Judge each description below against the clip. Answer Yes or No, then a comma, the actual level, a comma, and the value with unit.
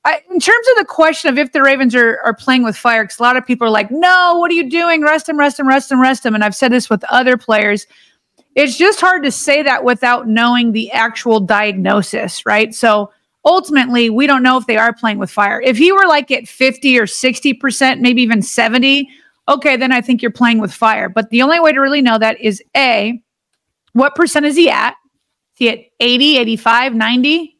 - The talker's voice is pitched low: No, very high, 255 Hz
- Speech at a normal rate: No, fast, 230 wpm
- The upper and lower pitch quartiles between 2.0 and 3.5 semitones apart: No, average, 4.0 semitones